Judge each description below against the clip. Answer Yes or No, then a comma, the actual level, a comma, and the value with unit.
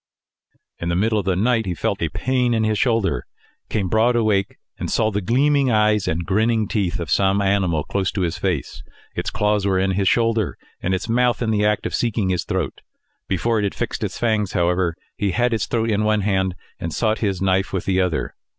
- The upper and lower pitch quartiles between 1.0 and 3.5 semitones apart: Yes, average, 3.0 semitones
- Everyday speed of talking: No, fast, 220 wpm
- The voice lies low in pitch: Yes, low, 105 Hz